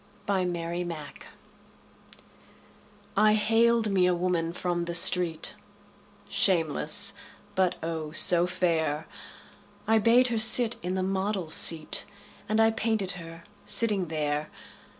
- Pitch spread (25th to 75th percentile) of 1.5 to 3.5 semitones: No, average, 4.1 semitones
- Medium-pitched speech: Yes, medium, 180 Hz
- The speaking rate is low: Yes, slow, 115 wpm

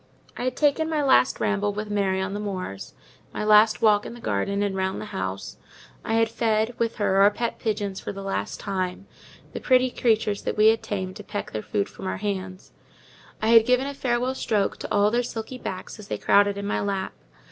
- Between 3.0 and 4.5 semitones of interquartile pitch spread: No, narrow, 2.6 semitones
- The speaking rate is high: Yes, fast, 215 wpm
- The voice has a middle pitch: No, high, 210 Hz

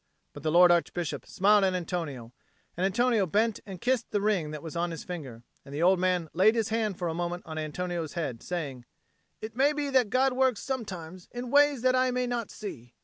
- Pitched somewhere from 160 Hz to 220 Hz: Yes, medium, 185 Hz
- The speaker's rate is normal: No, fast, 215 wpm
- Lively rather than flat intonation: Yes, wide, 6.1 semitones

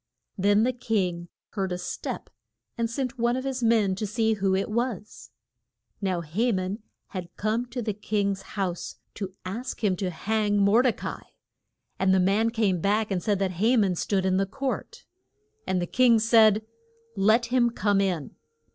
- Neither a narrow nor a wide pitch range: Yes, average, 3.3 semitones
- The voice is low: No, high, 210 Hz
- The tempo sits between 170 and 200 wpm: Yes, average, 180 wpm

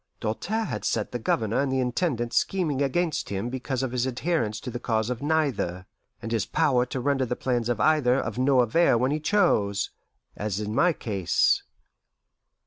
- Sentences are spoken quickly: No, average, 185 wpm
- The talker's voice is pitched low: Yes, low, 125 Hz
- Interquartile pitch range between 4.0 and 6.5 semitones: Yes, average, 4.3 semitones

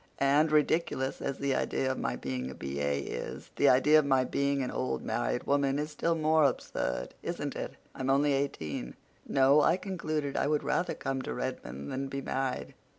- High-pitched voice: No, low, 135 Hz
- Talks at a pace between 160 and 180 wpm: No, average, 190 wpm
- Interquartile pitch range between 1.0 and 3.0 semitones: Yes, narrow, 2.6 semitones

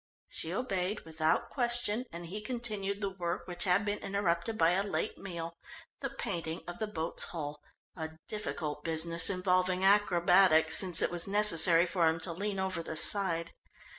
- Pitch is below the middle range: No, medium, 180 Hz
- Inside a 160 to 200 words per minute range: Yes, average, 165 wpm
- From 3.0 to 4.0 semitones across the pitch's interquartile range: Yes, average, 3.4 semitones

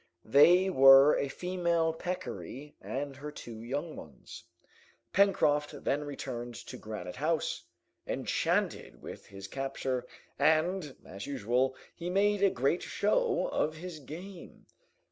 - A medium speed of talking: No, slow, 125 wpm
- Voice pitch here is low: No, medium, 145 Hz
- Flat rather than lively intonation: No, average, 5.1 semitones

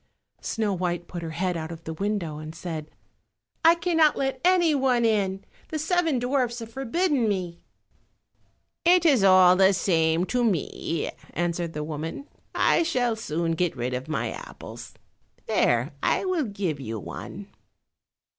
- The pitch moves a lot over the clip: Yes, wide, 8.3 semitones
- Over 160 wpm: No, average, 155 wpm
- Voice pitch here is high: Yes, high, 195 Hz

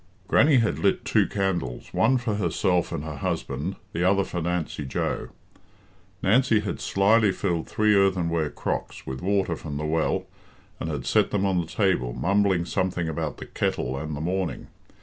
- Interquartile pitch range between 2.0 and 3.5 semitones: No, average, 4.0 semitones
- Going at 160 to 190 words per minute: Yes, average, 170 wpm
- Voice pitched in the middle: No, very low, 90 Hz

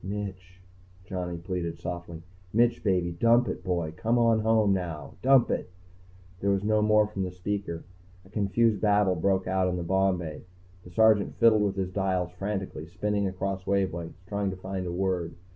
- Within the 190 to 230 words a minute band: No, average, 175 wpm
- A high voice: No, very low, 95 Hz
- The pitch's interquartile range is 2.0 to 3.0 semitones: Yes, narrow, 2.5 semitones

